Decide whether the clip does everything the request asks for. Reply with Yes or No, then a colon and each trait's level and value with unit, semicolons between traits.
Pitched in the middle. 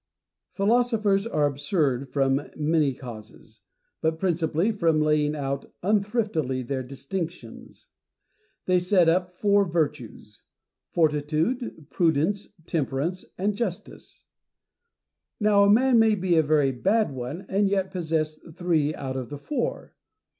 Yes: medium, 165 Hz